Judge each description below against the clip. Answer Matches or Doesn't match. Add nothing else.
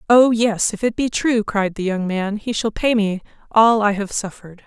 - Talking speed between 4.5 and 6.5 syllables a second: Matches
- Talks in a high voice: Matches